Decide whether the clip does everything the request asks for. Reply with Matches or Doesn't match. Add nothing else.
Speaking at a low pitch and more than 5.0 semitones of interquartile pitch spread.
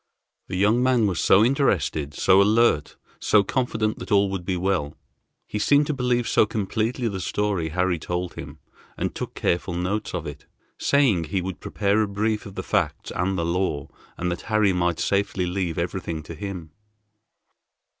Doesn't match